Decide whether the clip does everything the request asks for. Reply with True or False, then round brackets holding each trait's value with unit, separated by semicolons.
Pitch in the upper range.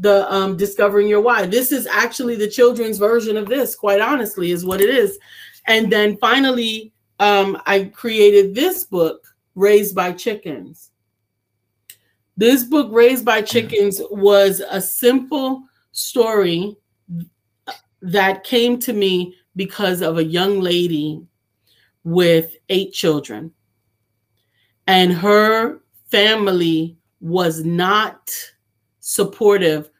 True (195 Hz)